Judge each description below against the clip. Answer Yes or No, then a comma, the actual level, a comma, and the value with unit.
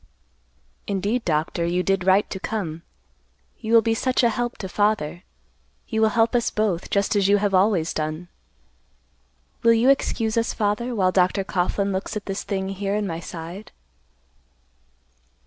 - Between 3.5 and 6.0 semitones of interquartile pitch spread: No, average, 3.1 semitones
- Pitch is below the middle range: No, high, 200 Hz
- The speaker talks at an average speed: Yes, average, 165 wpm